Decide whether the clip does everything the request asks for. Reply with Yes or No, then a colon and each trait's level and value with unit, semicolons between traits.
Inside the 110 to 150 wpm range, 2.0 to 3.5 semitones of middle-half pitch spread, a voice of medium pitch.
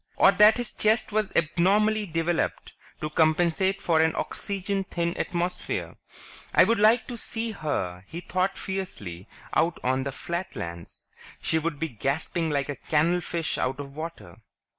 No: average, 145 wpm; average, 4.7 semitones; medium, 170 Hz